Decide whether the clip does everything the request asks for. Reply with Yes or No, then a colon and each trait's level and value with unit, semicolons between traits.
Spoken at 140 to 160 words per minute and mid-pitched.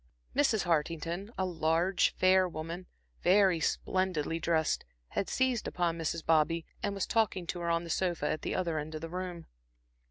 No: average, 170 wpm; medium, 175 Hz